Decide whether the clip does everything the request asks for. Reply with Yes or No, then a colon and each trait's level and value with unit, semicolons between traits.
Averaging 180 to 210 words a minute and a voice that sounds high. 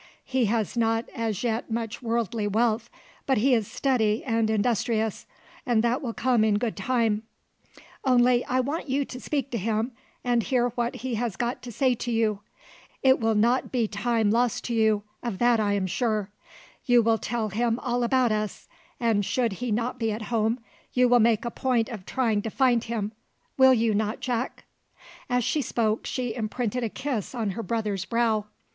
Yes: average, 190 wpm; high, 230 Hz